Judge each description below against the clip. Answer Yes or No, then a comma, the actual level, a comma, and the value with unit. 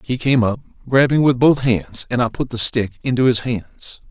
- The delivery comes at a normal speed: No, fast, 220 wpm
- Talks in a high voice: No, low, 120 Hz